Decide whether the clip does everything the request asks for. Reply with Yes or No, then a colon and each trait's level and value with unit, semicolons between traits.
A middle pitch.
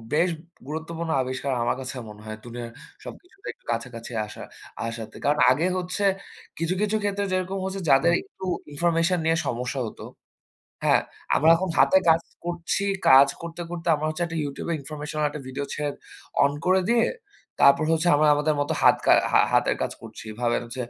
Yes: medium, 155 Hz